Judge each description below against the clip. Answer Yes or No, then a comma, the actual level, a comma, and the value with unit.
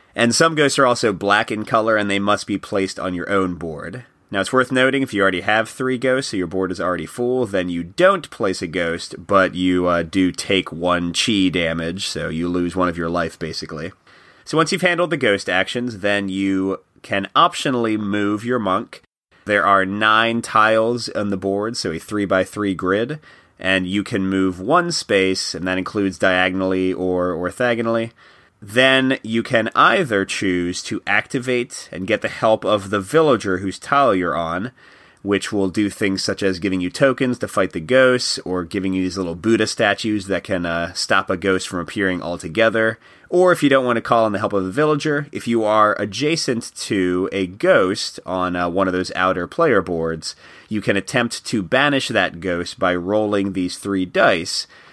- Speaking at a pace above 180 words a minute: Yes, average, 200 wpm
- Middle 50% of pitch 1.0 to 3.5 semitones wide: No, average, 3.9 semitones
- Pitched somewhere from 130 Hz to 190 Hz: No, low, 100 Hz